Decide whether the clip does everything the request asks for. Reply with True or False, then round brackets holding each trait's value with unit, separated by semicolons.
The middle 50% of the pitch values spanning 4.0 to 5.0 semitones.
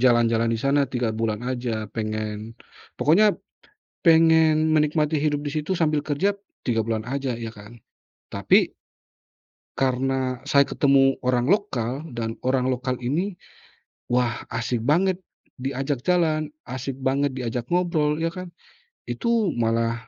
True (4.6 semitones)